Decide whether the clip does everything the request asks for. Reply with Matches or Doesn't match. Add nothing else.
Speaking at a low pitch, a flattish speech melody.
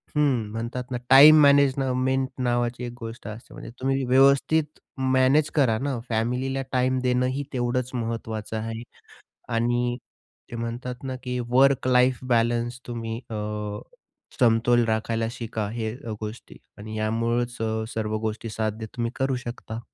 Matches